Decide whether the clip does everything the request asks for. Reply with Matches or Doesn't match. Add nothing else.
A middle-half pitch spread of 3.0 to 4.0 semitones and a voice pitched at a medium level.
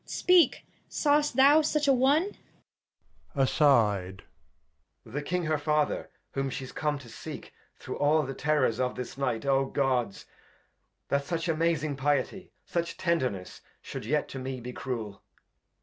Doesn't match